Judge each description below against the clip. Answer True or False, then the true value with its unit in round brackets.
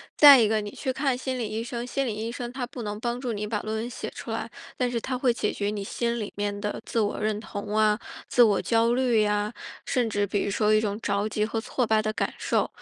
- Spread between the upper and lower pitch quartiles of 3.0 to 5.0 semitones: False (2.5 semitones)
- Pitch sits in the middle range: False (220 Hz)